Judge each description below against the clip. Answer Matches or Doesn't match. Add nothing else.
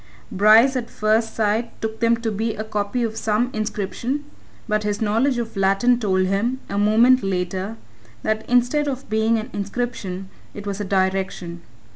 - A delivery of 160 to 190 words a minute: Matches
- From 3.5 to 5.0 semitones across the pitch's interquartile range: Doesn't match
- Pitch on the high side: Matches